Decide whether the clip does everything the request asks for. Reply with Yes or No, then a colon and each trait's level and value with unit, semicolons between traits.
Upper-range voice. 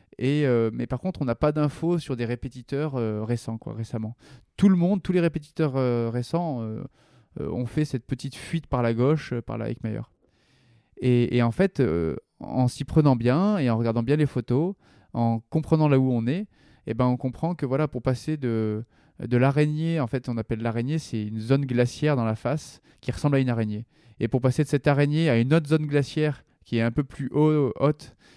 No: low, 130 Hz